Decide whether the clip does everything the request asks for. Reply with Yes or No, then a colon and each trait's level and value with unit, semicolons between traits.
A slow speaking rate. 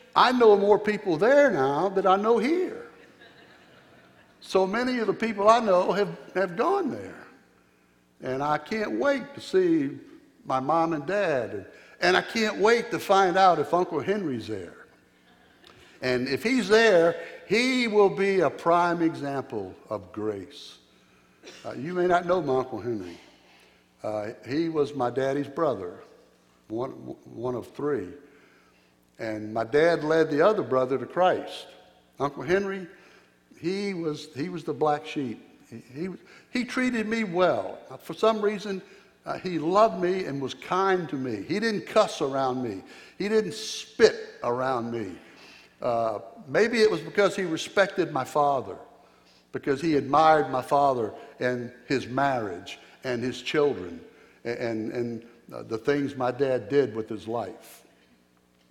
No: average, 155 wpm